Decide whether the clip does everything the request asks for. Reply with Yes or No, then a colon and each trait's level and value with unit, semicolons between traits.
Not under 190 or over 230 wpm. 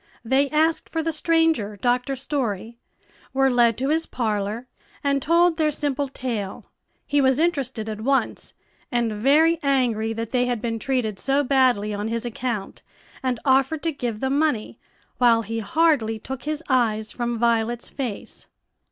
No: average, 160 wpm